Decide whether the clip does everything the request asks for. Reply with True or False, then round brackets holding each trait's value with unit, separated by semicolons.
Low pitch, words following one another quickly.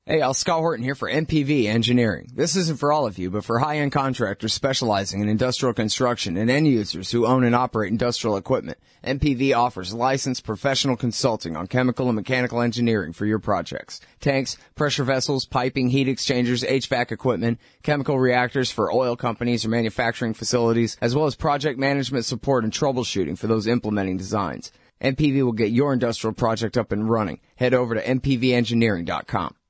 False (125 Hz; 170 wpm)